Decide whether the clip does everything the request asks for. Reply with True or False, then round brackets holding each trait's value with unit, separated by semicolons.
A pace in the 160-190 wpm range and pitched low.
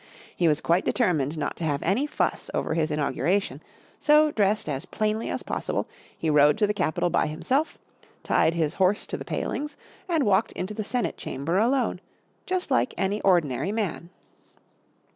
False (170 wpm; 190 Hz)